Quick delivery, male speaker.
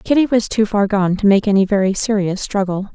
No: fast, 225 wpm; female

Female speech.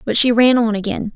Yes: female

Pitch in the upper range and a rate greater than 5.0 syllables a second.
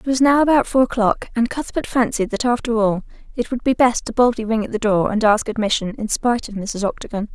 Yes: high, 230 Hz; 5.9 syllables/s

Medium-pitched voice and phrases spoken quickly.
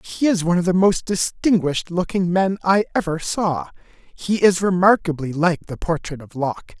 No: medium, 175 Hz; average, 175 wpm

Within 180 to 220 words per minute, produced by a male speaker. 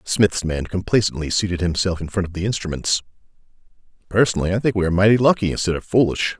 Yes: average, 190 wpm; male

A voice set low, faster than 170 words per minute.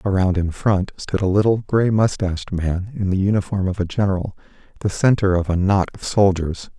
Yes: very low, 95 Hz; average, 195 wpm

